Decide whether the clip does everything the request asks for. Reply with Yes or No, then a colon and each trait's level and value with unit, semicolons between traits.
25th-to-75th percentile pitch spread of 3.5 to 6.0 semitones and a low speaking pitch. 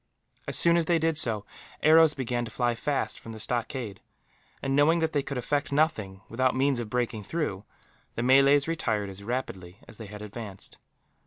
Yes: average, 5.3 semitones; low, 125 Hz